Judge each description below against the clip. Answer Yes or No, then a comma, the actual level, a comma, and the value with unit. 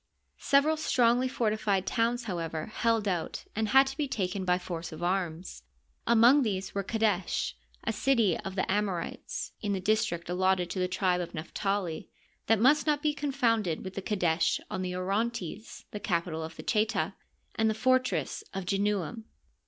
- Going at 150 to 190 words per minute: Yes, average, 165 wpm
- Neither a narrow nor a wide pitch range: Yes, average, 4.3 semitones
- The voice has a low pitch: No, high, 200 Hz